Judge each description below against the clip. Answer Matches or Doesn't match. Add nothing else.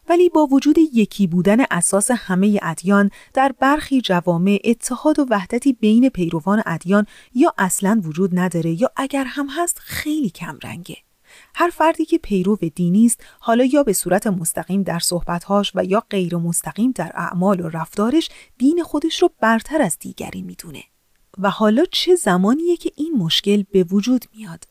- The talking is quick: Matches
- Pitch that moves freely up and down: Matches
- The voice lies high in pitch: Matches